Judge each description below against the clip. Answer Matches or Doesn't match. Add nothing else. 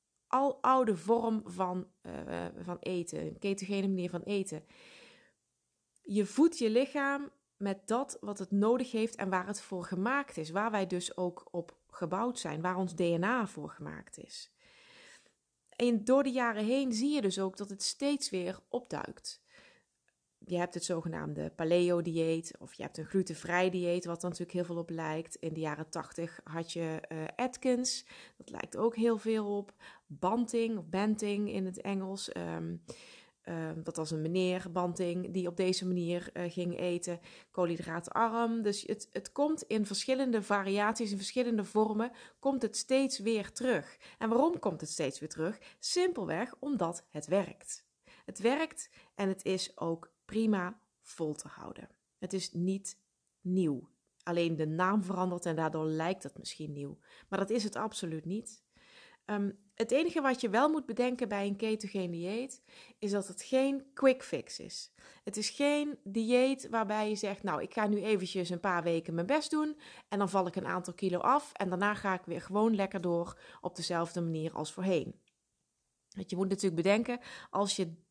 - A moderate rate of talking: Matches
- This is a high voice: Matches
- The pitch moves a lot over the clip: Doesn't match